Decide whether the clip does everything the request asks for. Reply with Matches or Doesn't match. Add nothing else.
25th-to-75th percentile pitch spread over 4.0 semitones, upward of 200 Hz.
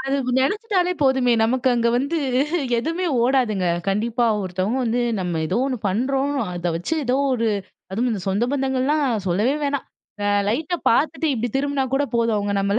Matches